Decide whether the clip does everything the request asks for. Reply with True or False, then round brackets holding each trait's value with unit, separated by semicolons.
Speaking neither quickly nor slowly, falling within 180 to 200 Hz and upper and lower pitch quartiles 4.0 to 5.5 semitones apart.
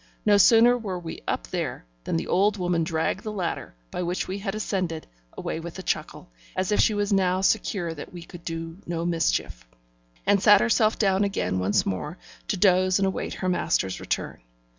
False (195 wpm; 185 Hz; 3.3 semitones)